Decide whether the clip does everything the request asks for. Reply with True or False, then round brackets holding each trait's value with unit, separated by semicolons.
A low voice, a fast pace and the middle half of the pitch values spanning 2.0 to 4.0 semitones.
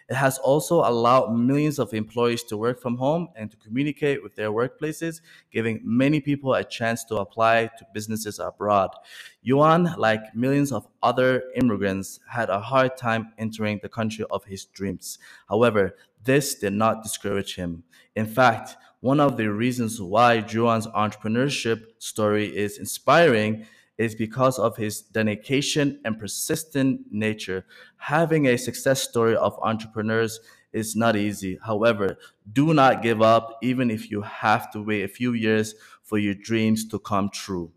False (115 Hz; 155 wpm; 3.3 semitones)